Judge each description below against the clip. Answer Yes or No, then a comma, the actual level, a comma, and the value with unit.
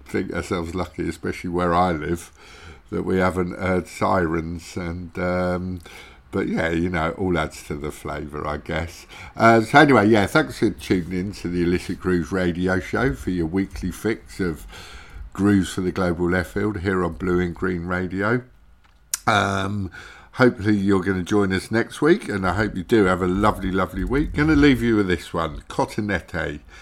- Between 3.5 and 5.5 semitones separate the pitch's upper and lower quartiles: No, average, 2.8 semitones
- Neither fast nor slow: Yes, average, 185 wpm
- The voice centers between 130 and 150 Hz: No, very low, 90 Hz